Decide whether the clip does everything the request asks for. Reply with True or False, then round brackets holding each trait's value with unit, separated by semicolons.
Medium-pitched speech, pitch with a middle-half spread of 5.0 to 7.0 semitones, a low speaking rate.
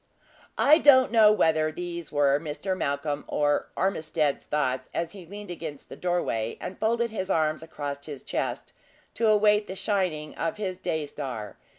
False (165 Hz; 5.5 semitones; 170 wpm)